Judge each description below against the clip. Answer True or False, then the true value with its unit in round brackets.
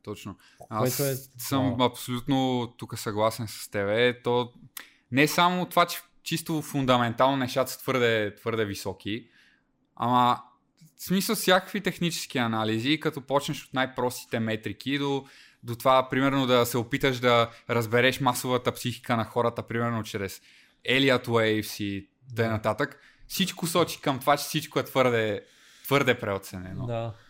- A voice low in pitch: True (125 Hz)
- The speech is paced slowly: False (140 wpm)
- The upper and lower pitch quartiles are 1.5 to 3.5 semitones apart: True (3.2 semitones)